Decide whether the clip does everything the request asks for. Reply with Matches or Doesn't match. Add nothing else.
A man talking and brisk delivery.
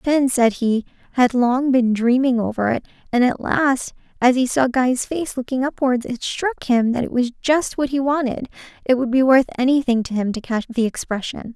Doesn't match